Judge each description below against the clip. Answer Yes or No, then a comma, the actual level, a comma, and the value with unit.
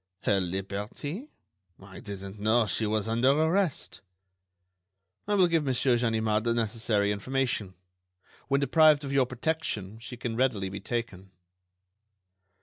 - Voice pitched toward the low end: Yes, low, 115 Hz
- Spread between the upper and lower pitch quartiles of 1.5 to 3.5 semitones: No, average, 5.1 semitones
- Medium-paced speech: No, slow, 130 wpm